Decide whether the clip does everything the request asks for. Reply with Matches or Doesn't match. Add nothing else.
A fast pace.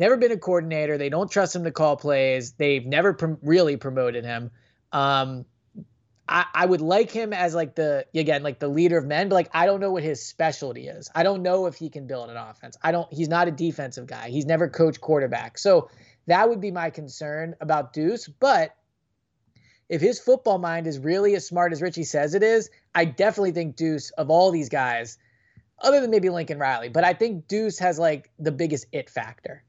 Matches